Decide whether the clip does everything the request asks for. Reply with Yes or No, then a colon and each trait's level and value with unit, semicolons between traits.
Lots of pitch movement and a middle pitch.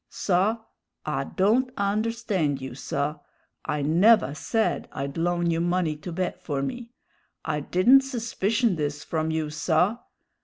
Yes: wide, 6.5 semitones; medium, 175 Hz